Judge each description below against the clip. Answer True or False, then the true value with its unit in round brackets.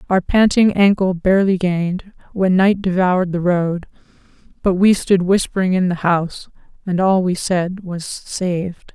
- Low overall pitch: False (185 Hz)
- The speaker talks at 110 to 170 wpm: True (155 wpm)